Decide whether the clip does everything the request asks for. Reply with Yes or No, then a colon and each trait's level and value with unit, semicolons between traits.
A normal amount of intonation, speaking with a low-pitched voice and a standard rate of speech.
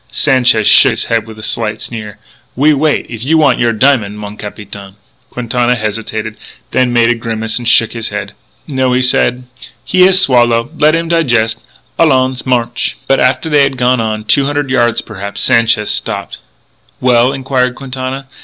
Yes: average, 3.1 semitones; low, 120 Hz; average, 170 wpm